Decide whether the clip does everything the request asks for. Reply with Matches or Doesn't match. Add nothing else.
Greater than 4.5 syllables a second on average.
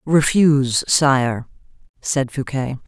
Doesn't match